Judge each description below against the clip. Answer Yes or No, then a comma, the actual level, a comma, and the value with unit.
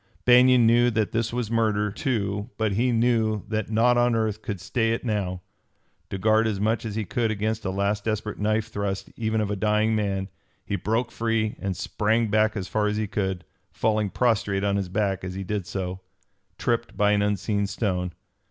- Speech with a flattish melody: Yes, narrow, 2.0 semitones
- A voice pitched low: Yes, low, 105 Hz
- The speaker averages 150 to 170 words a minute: No, average, 200 wpm